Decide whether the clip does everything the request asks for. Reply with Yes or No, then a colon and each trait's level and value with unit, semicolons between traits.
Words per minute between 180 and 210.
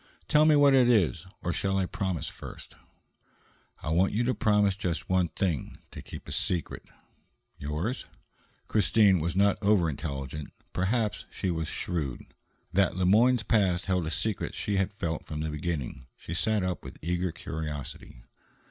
No: average, 165 wpm